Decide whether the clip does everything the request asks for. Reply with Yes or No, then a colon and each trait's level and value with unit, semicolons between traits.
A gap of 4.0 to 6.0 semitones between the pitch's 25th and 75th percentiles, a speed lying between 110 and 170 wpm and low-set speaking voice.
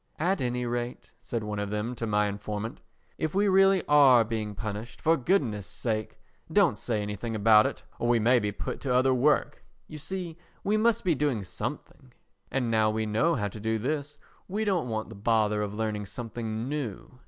No: wide, 5.5 semitones; average, 195 wpm; low, 120 Hz